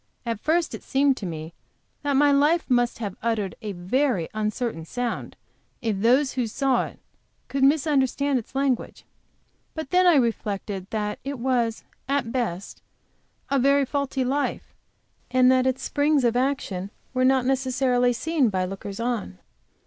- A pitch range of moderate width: Yes, average, 4.3 semitones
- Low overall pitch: No, very high, 255 Hz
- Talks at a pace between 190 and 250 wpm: No, average, 155 wpm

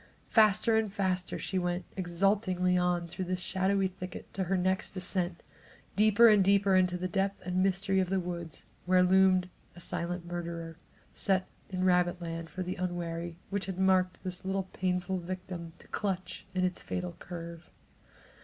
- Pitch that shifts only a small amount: Yes, narrow, 1.3 semitones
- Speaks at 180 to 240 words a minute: No, average, 170 wpm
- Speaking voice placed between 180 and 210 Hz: Yes, medium, 185 Hz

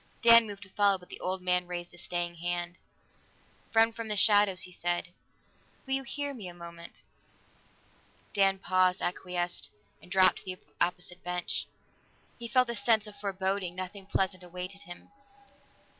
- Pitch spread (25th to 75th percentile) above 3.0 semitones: No, narrow, 2.5 semitones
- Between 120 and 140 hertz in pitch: No, medium, 185 Hz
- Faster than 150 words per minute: Yes, average, 160 wpm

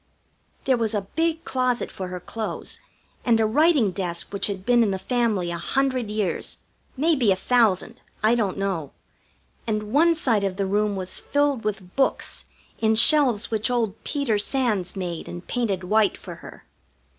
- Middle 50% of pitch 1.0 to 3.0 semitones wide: No, average, 4.3 semitones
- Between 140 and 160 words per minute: No, average, 170 wpm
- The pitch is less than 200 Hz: No, high, 220 Hz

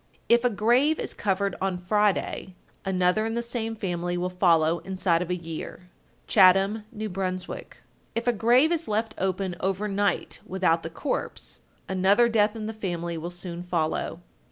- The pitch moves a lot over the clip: No, average, 3.4 semitones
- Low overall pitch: No, high, 190 Hz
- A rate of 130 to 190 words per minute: Yes, average, 165 wpm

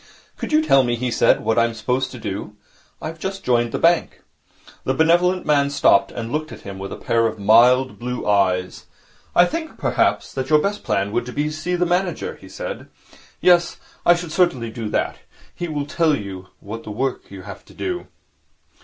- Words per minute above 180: Yes, average, 195 wpm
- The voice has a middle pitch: No, low, 130 Hz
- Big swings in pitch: Yes, wide, 7.5 semitones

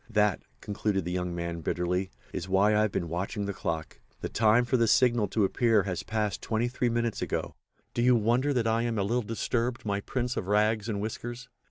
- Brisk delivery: Yes, fast, 215 wpm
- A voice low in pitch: Yes, low, 110 Hz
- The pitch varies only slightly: No, average, 3.3 semitones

